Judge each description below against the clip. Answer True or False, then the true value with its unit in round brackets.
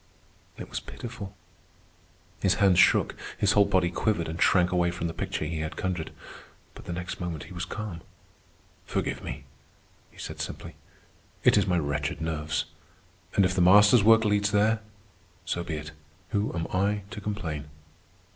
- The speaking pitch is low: True (90 Hz)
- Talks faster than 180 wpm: False (165 wpm)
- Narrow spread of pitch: False (3.8 semitones)